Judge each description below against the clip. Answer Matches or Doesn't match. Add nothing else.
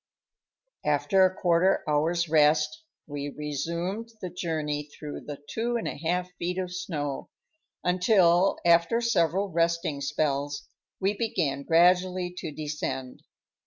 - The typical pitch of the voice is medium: Matches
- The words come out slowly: Matches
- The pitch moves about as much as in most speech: Matches